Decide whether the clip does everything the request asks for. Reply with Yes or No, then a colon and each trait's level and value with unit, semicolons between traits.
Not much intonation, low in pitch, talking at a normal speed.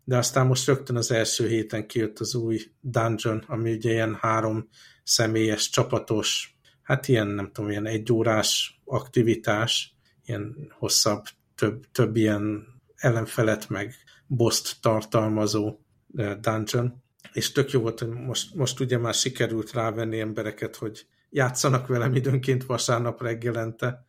Yes: narrow, 2.2 semitones; low, 115 Hz; average, 130 wpm